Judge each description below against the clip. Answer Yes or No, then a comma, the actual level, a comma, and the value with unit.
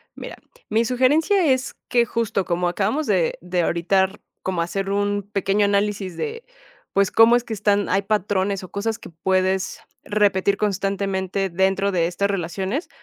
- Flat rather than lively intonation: Yes, narrow, 2.1 semitones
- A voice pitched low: No, high, 200 Hz